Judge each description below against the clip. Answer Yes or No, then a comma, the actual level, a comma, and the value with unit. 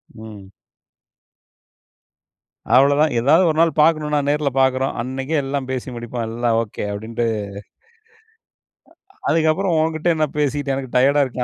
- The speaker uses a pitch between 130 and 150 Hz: Yes, low, 135 Hz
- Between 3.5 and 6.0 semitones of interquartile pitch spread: Yes, average, 4.1 semitones